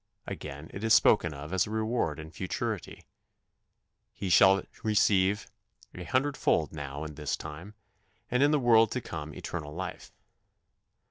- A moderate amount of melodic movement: No, wide, 6.1 semitones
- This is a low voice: Yes, very low, 95 Hz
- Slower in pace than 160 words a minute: Yes, average, 150 wpm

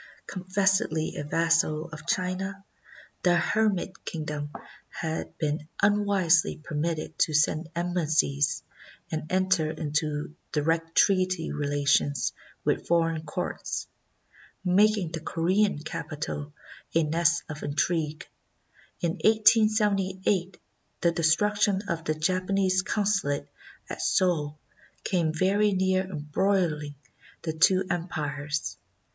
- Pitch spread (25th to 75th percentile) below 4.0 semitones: Yes, average, 3.5 semitones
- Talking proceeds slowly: Yes, slow, 105 wpm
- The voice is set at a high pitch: No, medium, 170 Hz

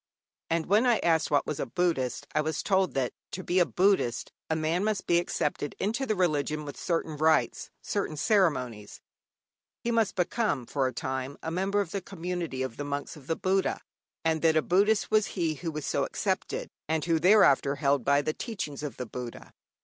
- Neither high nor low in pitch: Yes, medium, 160 Hz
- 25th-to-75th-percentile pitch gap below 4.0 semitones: No, average, 4.8 semitones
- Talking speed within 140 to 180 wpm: No, average, 200 wpm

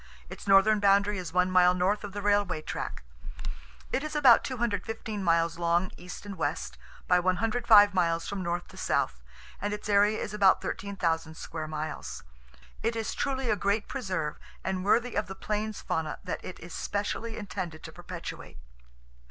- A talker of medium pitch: No, high, 195 Hz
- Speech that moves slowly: No, average, 170 wpm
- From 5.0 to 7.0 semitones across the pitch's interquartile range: No, average, 3.2 semitones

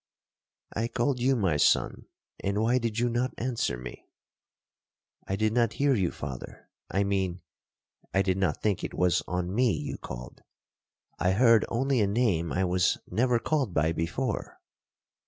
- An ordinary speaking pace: Yes, average, 155 wpm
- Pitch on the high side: No, low, 105 Hz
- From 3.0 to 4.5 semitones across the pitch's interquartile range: No, average, 5.0 semitones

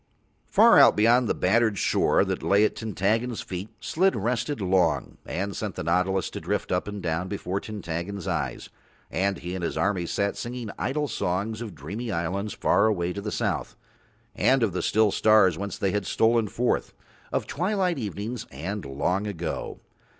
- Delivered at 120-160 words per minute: No, average, 180 wpm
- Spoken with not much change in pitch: No, average, 3.5 semitones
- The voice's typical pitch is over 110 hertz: No, low, 100 Hz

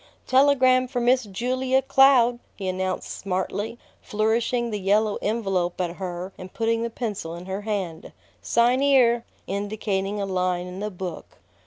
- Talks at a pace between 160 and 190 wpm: No, average, 150 wpm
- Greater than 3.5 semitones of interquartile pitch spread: Yes, average, 4.3 semitones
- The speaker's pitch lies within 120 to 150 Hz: No, high, 210 Hz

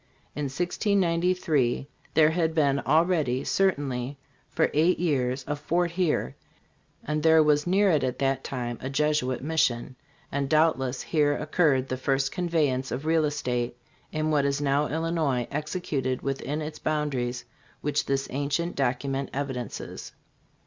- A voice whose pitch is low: No, medium, 145 Hz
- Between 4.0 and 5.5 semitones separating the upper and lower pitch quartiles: No, average, 3.3 semitones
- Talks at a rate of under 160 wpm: Yes, average, 140 wpm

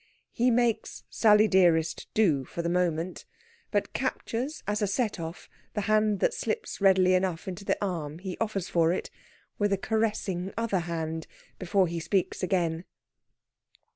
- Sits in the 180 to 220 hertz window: Yes, high, 190 Hz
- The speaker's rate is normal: Yes, average, 155 wpm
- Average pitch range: Yes, average, 3.9 semitones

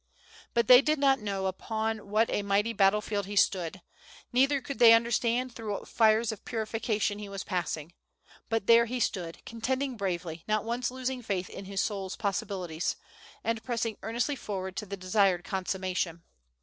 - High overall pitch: Yes, high, 210 Hz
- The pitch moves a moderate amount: Yes, average, 3.4 semitones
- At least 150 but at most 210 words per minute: Yes, average, 170 wpm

